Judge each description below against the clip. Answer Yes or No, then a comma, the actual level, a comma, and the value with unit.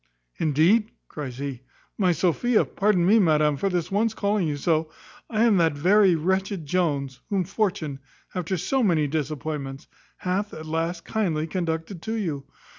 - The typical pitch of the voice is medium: Yes, medium, 170 Hz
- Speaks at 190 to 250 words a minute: No, average, 155 wpm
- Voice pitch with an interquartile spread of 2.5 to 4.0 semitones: No, average, 4.6 semitones